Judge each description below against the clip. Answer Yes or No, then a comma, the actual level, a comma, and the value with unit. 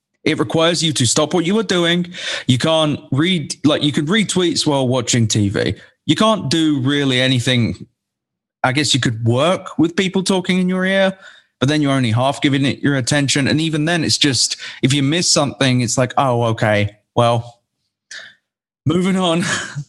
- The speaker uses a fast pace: No, average, 185 wpm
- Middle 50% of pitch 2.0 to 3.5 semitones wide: No, average, 5.1 semitones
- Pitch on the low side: No, medium, 145 Hz